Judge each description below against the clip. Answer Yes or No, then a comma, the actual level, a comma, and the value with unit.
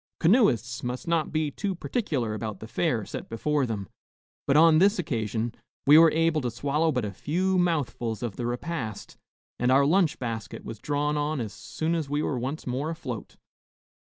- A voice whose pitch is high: No, medium, 145 Hz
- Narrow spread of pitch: No, wide, 5.6 semitones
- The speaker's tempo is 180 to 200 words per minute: Yes, average, 185 wpm